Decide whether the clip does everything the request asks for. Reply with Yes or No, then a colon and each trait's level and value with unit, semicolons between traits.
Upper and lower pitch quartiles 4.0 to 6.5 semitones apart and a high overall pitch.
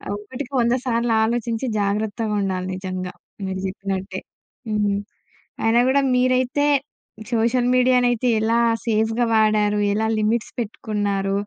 No: average, 2.9 semitones; high, 220 Hz